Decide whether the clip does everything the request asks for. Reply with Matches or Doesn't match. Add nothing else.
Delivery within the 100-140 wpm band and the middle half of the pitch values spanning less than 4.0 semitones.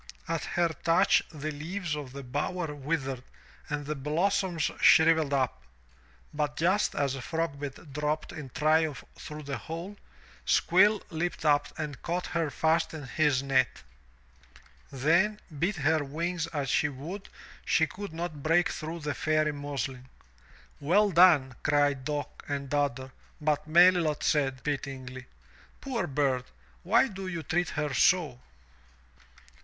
Matches